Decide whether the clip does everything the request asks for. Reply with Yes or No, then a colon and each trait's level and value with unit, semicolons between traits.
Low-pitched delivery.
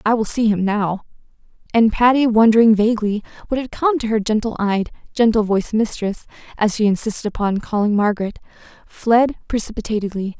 No: high, 220 Hz